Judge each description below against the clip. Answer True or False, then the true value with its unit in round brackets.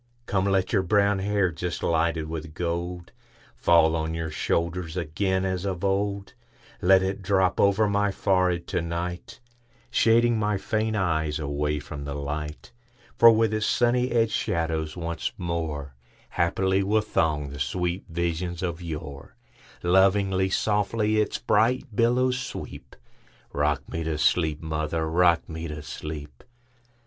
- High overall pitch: False (90 Hz)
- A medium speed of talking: False (125 wpm)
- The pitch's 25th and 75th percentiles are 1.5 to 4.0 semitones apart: False (4.4 semitones)